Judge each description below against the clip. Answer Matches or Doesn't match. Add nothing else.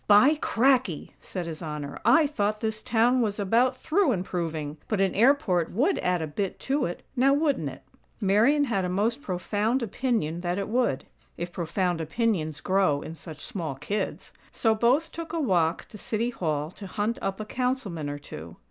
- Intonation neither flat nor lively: Doesn't match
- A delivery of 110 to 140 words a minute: Doesn't match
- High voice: Matches